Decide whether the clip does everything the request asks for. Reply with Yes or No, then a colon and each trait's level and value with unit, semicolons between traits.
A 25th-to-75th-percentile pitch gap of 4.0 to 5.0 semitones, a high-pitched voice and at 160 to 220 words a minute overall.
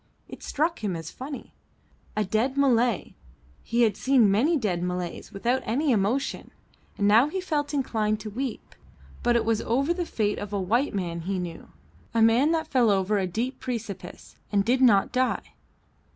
Yes: average, 4.7 semitones; high, 230 Hz; average, 180 wpm